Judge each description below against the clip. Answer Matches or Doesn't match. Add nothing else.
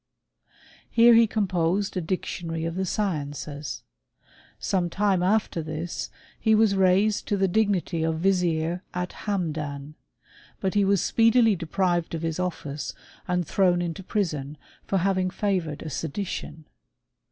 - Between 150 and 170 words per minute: Doesn't match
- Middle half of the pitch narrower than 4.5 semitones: Matches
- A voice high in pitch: Doesn't match